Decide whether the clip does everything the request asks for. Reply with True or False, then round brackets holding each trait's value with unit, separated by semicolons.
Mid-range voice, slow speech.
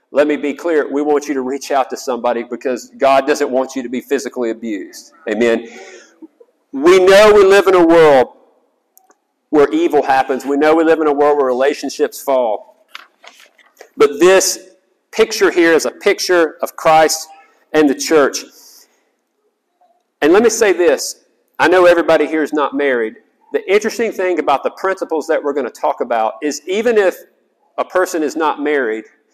False (170 Hz; 175 wpm)